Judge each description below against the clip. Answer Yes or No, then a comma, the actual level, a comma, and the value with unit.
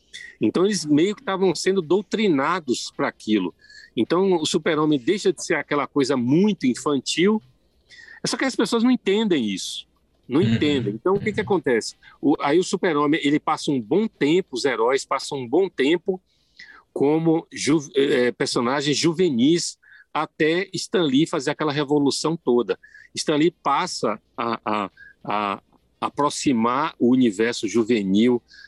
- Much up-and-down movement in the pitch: Yes, wide, 7.1 semitones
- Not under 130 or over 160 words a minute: Yes, average, 150 wpm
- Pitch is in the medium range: Yes, medium, 165 Hz